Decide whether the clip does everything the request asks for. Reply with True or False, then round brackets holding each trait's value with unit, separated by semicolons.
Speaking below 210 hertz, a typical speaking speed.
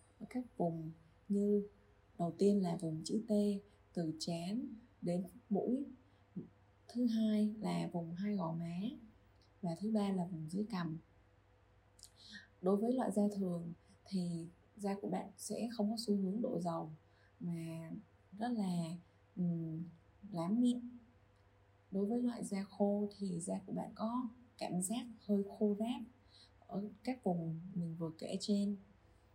False (190 Hz; 145 wpm)